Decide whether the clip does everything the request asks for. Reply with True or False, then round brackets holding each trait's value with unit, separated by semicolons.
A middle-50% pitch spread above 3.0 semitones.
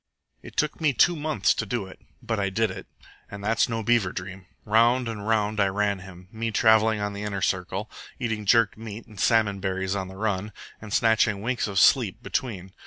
False (2.6 semitones)